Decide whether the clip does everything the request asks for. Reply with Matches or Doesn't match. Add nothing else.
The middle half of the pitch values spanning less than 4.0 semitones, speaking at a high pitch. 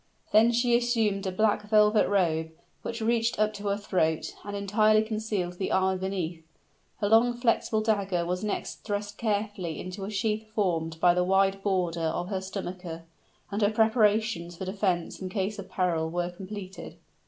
Matches